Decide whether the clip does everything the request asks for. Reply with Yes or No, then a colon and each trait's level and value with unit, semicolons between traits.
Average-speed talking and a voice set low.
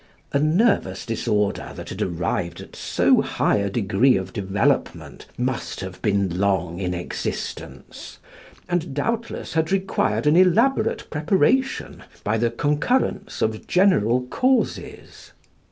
No: slow, 120 wpm; low, 125 Hz